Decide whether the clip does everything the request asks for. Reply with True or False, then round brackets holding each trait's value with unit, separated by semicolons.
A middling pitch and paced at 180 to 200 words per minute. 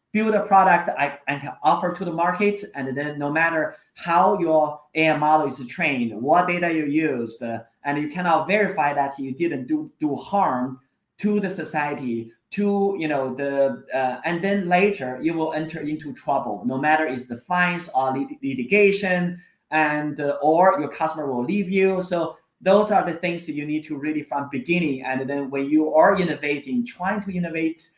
True (155 Hz; 185 wpm)